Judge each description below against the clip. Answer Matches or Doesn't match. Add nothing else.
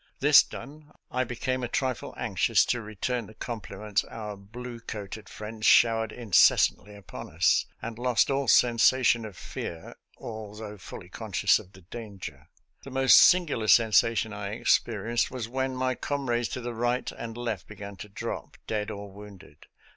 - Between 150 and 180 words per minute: Matches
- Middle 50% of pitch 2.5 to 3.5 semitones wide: Matches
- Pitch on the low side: Matches